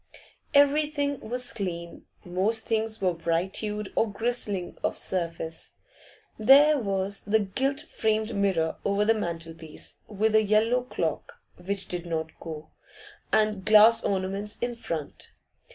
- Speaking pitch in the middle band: No, high, 210 Hz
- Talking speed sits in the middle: No, slow, 130 wpm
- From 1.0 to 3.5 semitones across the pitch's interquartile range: No, average, 4.1 semitones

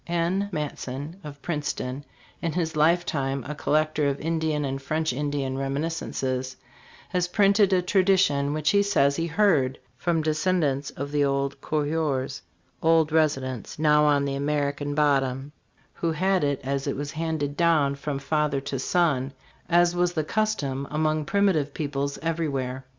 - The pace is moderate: Yes, average, 150 wpm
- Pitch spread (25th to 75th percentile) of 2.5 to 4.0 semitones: Yes, average, 3.0 semitones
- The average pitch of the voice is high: No, medium, 150 Hz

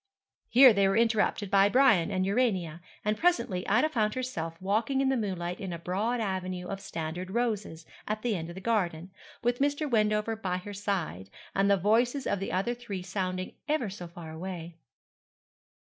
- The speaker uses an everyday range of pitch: Yes, average, 4.2 semitones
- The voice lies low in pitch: No, high, 200 Hz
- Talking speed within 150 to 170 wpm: No, average, 180 wpm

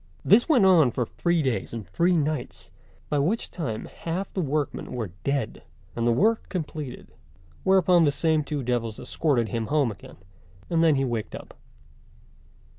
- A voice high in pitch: No, medium, 150 Hz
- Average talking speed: Yes, average, 165 wpm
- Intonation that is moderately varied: No, wide, 5.9 semitones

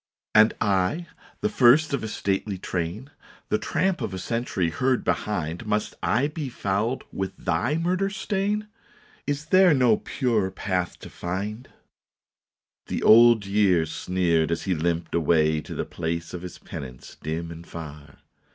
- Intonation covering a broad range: Yes, wide, 7.5 semitones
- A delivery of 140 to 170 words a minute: Yes, average, 160 wpm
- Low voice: Yes, low, 100 Hz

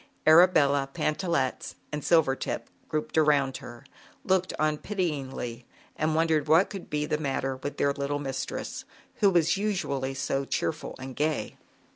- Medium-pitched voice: Yes, medium, 150 Hz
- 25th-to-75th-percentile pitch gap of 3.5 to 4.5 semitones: No, average, 3.1 semitones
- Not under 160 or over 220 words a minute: No, average, 145 wpm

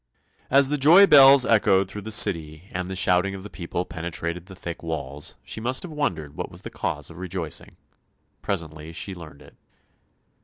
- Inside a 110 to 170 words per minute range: No, average, 185 wpm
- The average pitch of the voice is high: No, very low, 90 Hz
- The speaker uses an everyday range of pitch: Yes, average, 5.0 semitones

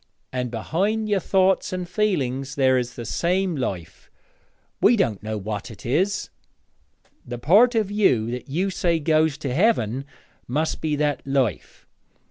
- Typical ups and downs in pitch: No, wide, 7.5 semitones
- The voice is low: No, medium, 150 Hz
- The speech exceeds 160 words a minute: No, average, 150 wpm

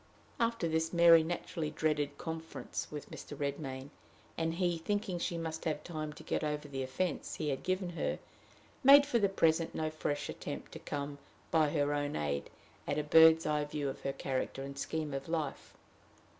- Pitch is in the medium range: Yes, medium, 155 Hz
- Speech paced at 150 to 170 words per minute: No, average, 185 wpm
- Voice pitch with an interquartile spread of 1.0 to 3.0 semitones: Yes, narrow, 2.5 semitones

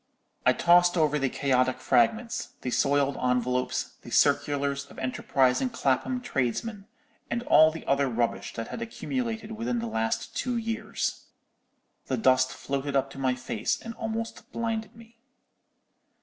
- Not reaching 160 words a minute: Yes, average, 145 wpm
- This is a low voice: No, medium, 145 Hz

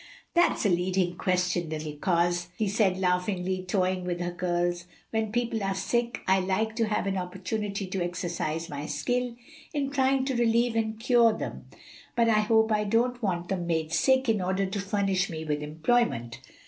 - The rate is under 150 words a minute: No, average, 180 wpm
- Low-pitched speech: No, high, 190 Hz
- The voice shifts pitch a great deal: No, average, 4.2 semitones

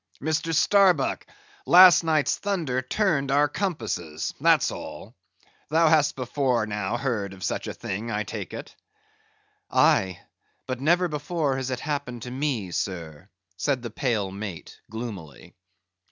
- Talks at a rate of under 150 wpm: Yes, slow, 135 wpm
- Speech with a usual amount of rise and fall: No, wide, 6.6 semitones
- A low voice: Yes, low, 130 Hz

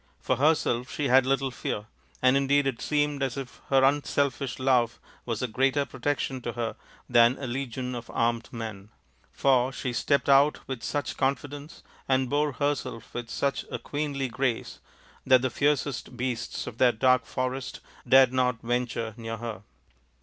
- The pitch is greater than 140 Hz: No, low, 130 Hz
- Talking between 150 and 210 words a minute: Yes, average, 165 wpm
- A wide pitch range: No, narrow, 2.5 semitones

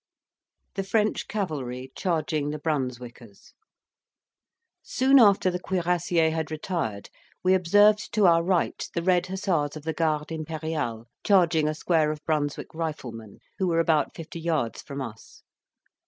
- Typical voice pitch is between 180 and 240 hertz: No, medium, 160 Hz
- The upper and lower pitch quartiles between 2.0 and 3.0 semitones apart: No, average, 3.5 semitones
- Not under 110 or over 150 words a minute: Yes, average, 140 wpm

